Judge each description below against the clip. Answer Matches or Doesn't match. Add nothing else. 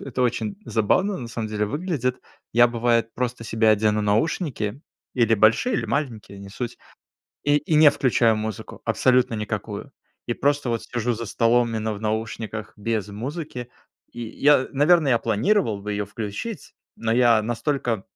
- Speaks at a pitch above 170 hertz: Doesn't match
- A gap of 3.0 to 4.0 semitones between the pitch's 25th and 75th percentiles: Matches